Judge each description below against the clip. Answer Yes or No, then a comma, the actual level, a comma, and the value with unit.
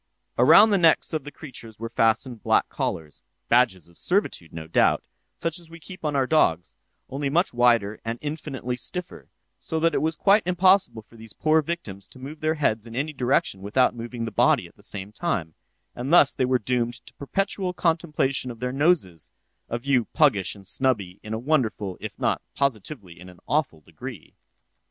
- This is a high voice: No, low, 125 Hz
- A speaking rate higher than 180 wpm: Yes, average, 190 wpm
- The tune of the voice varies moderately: No, wide, 6.1 semitones